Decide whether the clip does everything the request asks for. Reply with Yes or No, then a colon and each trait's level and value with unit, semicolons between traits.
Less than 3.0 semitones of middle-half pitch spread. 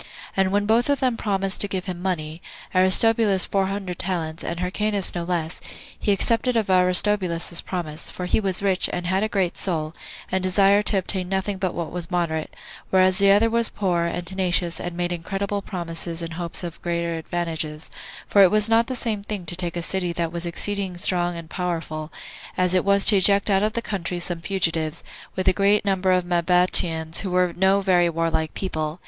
Yes: narrow, 2.6 semitones